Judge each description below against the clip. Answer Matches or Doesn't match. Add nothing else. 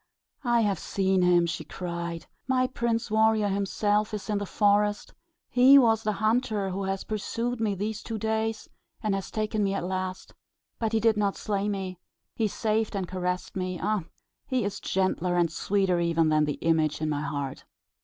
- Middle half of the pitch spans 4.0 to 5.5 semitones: Doesn't match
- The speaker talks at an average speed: Matches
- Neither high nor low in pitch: Doesn't match